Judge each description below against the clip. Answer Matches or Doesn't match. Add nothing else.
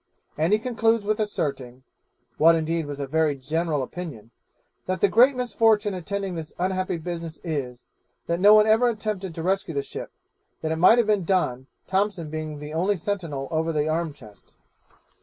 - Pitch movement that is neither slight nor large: Matches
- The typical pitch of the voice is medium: Matches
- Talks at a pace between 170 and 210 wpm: Matches